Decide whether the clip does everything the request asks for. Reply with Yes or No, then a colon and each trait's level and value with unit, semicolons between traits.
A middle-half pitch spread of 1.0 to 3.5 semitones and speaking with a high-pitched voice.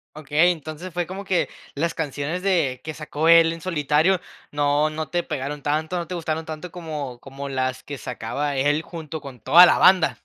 No: average, 2.8 semitones; medium, 155 Hz